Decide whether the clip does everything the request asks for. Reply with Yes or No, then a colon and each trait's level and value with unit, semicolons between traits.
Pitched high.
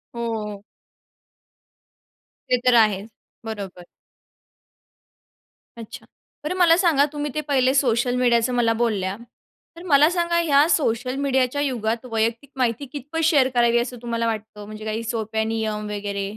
Yes: high, 235 Hz